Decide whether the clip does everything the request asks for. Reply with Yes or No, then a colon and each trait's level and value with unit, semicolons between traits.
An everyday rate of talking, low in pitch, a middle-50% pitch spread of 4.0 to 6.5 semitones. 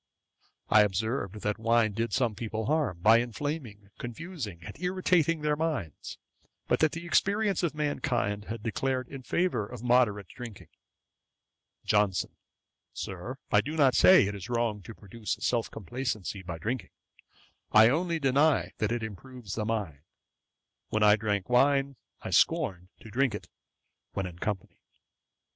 Yes: average, 150 wpm; low, 115 Hz; average, 5.1 semitones